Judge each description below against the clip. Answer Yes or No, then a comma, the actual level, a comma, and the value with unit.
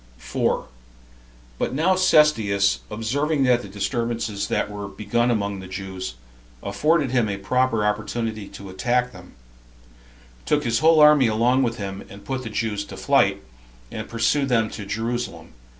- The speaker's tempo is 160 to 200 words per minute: No, average, 150 wpm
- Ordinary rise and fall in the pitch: Yes, average, 4.2 semitones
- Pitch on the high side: No, low, 115 Hz